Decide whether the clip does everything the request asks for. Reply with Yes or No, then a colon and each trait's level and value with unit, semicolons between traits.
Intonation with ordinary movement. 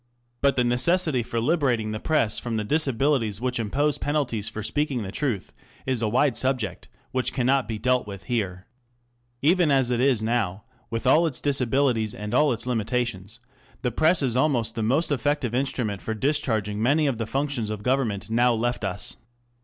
Yes: average, 4.0 semitones